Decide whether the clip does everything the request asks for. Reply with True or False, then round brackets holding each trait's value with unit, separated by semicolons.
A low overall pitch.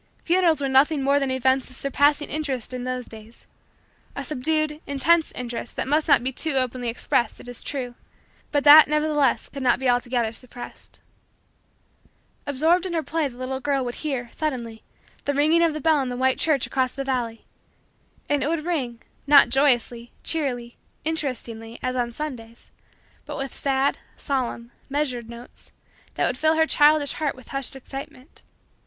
False (270 Hz)